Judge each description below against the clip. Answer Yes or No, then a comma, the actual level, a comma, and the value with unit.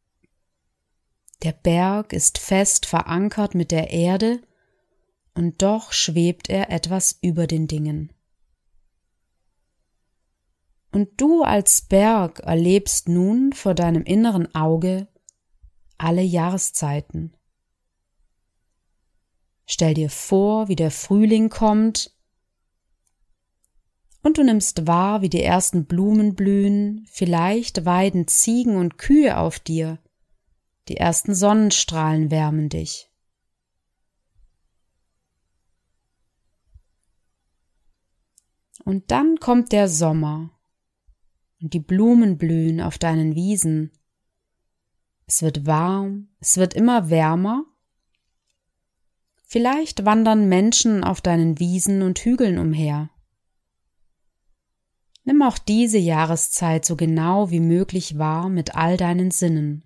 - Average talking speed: No, slow, 95 wpm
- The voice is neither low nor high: Yes, medium, 170 Hz